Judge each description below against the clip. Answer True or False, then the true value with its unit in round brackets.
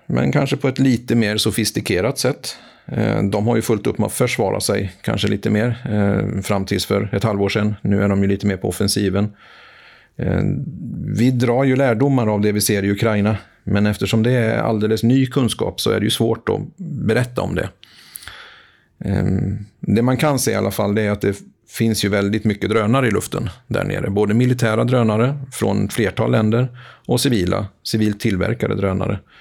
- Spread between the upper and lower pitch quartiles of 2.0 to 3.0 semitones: True (2.7 semitones)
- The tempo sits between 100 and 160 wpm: False (185 wpm)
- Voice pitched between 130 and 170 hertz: False (110 Hz)